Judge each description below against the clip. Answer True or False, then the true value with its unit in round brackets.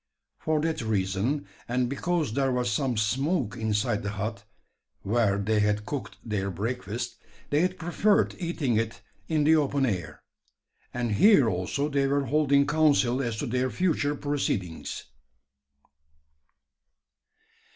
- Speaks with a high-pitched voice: False (125 Hz)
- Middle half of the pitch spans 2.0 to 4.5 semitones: False (5.4 semitones)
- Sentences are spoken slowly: True (130 wpm)